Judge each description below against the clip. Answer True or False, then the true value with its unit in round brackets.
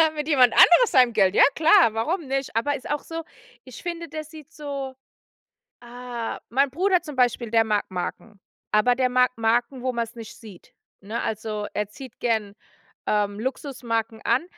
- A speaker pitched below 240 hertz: False (245 Hz)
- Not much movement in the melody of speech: False (4.4 semitones)